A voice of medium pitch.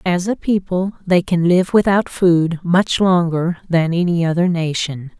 Yes: medium, 175 Hz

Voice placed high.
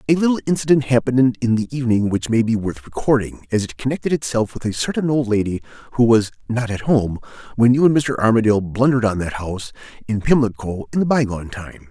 No: low, 120 Hz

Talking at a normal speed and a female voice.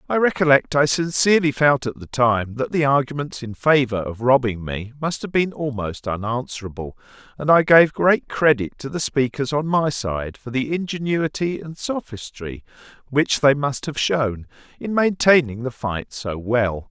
No: average, 170 wpm; male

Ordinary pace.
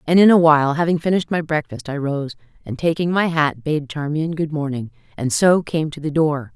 No: fast, 220 wpm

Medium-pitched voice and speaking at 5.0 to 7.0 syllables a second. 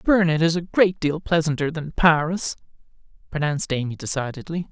Yes: medium, 160 Hz; 5.4 syllables/s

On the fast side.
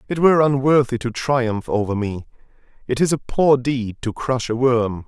No: average, 180 wpm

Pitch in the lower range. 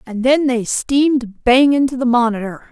No: very high, 250 Hz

